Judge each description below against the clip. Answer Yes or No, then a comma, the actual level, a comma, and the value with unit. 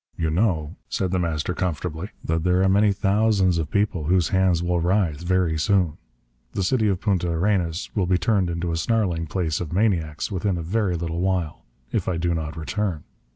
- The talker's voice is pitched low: Yes, very low, 90 Hz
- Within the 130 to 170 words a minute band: No, average, 195 wpm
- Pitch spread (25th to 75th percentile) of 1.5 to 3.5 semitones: Yes, average, 2.9 semitones